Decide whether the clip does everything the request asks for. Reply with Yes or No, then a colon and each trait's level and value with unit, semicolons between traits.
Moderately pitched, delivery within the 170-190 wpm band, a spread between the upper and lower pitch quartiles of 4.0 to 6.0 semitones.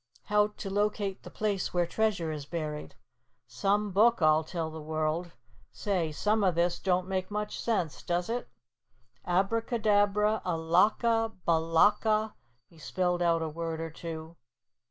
No: medium, 180 Hz; average, 145 wpm; average, 4.3 semitones